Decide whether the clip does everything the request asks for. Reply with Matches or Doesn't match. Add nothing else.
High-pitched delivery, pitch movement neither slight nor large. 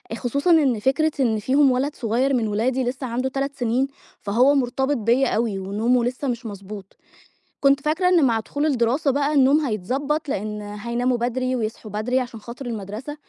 Matches